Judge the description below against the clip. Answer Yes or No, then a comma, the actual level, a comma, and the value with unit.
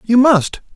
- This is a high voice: Yes, high, 235 Hz